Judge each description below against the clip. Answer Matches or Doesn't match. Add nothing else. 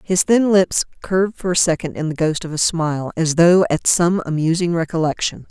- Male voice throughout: Doesn't match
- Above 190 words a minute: Matches